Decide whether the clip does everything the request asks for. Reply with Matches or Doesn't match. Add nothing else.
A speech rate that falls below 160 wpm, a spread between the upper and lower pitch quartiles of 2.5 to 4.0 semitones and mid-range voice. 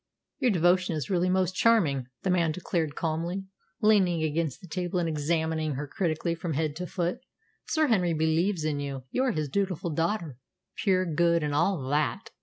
Doesn't match